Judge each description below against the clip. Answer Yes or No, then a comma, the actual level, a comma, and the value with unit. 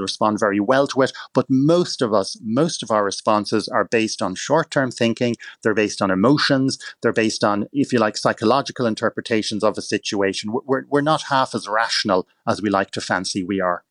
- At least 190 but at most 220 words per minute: Yes, fast, 205 wpm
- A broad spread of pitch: No, average, 4.1 semitones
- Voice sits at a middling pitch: No, low, 110 Hz